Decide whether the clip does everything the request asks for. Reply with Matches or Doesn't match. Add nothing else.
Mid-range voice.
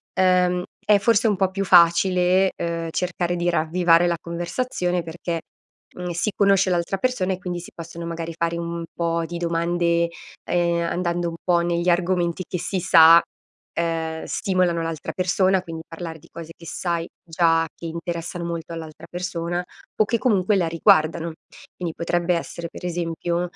Matches